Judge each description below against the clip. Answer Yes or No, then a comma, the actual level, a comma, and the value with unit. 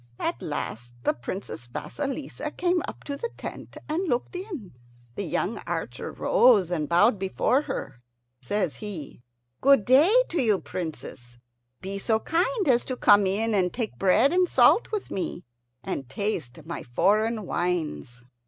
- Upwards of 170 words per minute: No, average, 155 wpm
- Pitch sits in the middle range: No, high, 210 Hz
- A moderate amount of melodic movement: No, wide, 8.2 semitones